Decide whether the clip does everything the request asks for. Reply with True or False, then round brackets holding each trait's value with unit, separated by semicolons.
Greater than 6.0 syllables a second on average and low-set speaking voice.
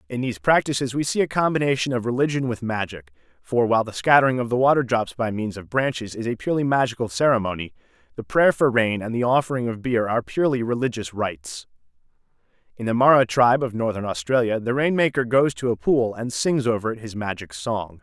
True (6.2 syllables/s; 120 Hz)